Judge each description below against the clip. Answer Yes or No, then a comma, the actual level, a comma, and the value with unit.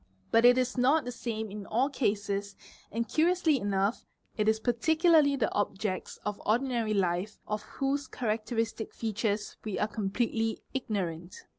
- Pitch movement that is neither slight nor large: Yes, average, 3.6 semitones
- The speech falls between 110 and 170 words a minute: Yes, average, 145 wpm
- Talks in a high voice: Yes, high, 220 Hz